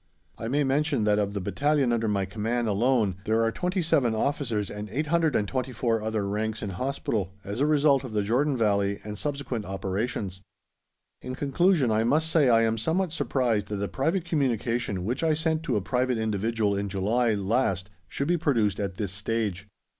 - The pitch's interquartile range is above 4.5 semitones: Yes, average, 5.2 semitones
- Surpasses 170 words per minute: Yes, average, 180 wpm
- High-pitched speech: No, low, 115 Hz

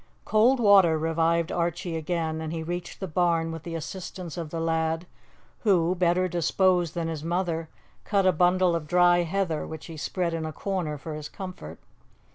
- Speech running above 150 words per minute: Yes, average, 180 wpm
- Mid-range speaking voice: Yes, medium, 170 Hz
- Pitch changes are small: Yes, narrow, 2.1 semitones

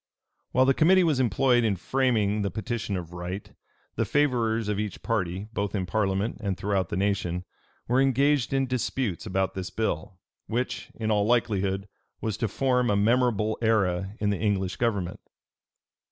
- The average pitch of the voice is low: Yes, low, 105 Hz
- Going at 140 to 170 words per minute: Yes, average, 165 wpm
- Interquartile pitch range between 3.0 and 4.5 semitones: Yes, average, 4.1 semitones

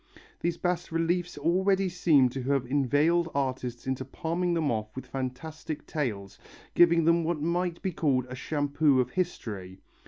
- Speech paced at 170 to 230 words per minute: No, average, 155 wpm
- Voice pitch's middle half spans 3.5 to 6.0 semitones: Yes, average, 4.9 semitones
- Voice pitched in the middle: Yes, medium, 150 Hz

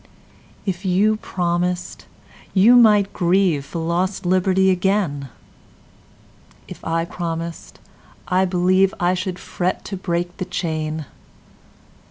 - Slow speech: Yes, slow, 95 wpm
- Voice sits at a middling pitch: Yes, medium, 180 Hz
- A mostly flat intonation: Yes, narrow, 1.9 semitones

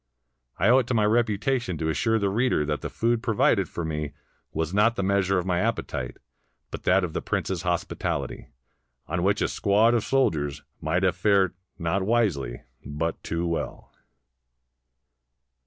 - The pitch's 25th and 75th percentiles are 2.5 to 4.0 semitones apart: No, wide, 5.6 semitones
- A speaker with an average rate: Yes, average, 165 wpm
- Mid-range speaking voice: No, very low, 95 Hz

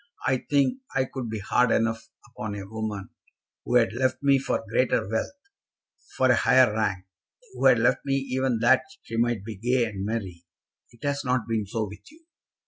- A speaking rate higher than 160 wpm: Yes, average, 190 wpm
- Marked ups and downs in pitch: No, average, 3.3 semitones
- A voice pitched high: No, low, 115 Hz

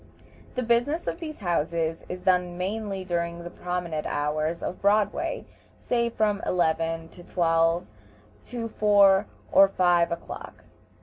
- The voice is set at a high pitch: No, medium, 180 Hz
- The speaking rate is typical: No, slow, 130 wpm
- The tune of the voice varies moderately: Yes, average, 3.6 semitones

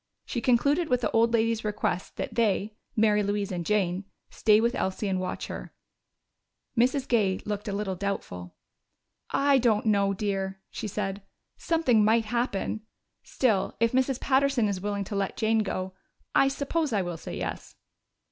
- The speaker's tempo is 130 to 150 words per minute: No, average, 165 wpm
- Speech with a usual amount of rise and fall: Yes, average, 3.3 semitones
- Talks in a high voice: Yes, high, 215 Hz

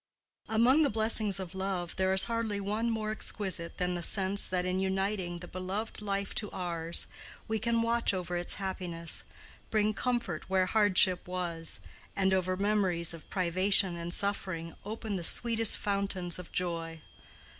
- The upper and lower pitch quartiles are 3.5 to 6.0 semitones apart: No, average, 3.0 semitones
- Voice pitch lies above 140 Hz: Yes, high, 190 Hz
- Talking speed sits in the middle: Yes, average, 155 wpm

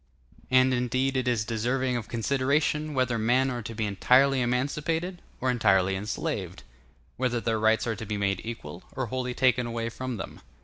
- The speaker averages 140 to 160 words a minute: No, average, 180 wpm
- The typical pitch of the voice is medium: No, low, 125 Hz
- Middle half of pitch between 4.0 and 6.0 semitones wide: No, average, 2.7 semitones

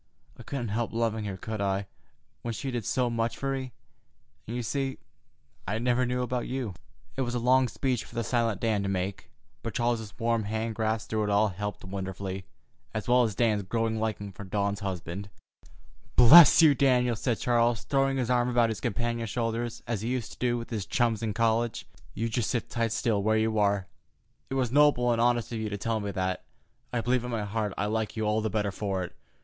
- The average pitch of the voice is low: Yes, low, 115 Hz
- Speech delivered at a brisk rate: Yes, fast, 215 wpm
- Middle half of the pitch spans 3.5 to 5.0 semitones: No, average, 2.7 semitones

